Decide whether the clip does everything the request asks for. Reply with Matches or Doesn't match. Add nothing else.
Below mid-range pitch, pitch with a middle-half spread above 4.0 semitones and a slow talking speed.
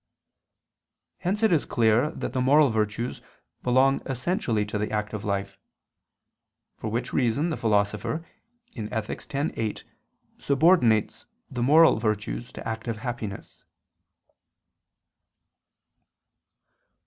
Matches